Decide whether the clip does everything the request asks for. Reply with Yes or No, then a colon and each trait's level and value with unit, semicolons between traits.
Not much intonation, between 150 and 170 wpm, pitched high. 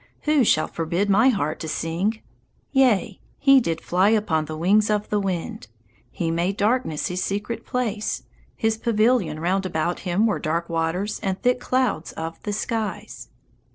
No: average, 4.8 semitones; average, 160 wpm; high, 200 Hz